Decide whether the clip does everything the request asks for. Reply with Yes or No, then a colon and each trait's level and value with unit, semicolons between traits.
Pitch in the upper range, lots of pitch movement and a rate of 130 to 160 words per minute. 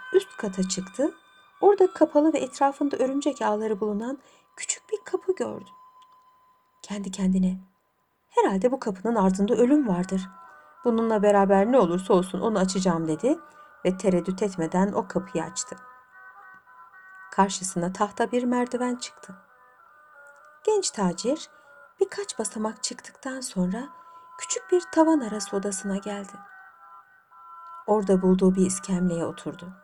No: high, 215 Hz; wide, 7.5 semitones; average, 115 wpm